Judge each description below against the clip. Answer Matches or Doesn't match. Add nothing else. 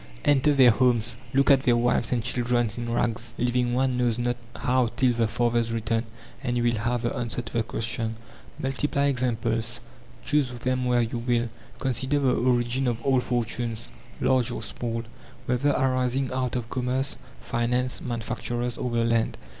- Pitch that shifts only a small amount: Matches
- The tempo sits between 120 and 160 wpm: Doesn't match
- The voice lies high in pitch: Doesn't match